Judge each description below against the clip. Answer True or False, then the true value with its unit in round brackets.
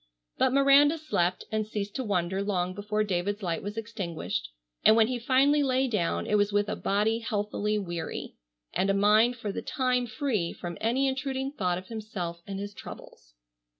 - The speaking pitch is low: False (210 Hz)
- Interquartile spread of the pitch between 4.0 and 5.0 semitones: True (4.7 semitones)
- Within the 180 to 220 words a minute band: True (185 wpm)